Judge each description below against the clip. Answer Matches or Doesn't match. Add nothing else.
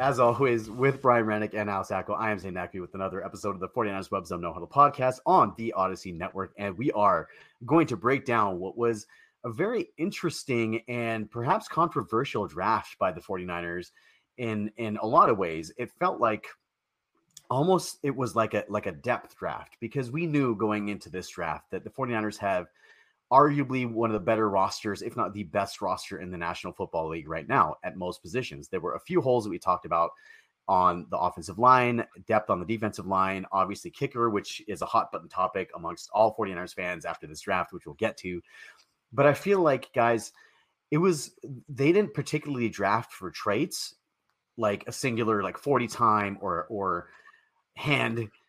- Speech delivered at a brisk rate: Doesn't match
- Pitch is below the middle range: Matches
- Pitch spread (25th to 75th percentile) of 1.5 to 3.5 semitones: Doesn't match